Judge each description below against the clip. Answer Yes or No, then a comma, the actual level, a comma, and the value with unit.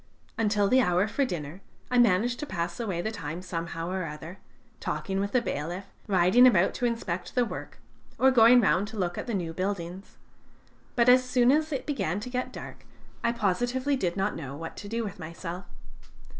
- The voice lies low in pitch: No, high, 200 Hz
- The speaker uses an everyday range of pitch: No, wide, 5.7 semitones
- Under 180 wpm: No, average, 195 wpm